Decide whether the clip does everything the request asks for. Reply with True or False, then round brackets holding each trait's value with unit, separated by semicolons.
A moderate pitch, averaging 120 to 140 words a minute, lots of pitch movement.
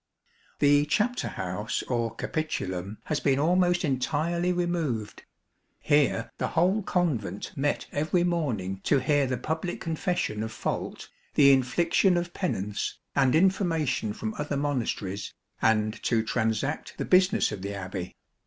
True (145 Hz; 135 wpm; 7.7 semitones)